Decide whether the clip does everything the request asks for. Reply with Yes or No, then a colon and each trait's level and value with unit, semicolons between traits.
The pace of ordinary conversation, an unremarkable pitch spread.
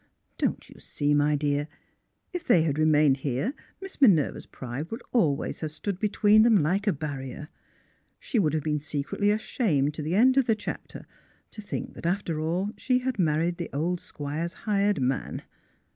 No: average, 175 wpm; wide, 5.9 semitones